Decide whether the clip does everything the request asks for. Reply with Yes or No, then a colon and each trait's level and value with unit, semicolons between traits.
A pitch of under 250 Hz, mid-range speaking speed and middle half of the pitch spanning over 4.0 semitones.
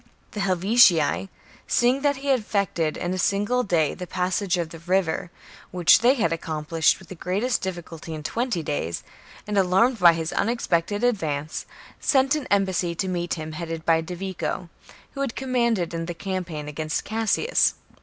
Yes: medium, 185 Hz; average, 165 wpm; average, 5.1 semitones